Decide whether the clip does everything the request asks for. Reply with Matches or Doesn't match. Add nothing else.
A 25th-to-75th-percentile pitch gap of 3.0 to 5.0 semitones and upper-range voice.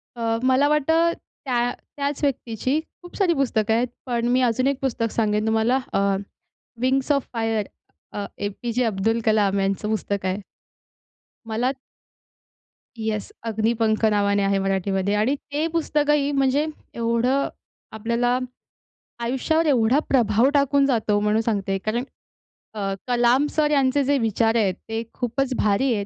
Matches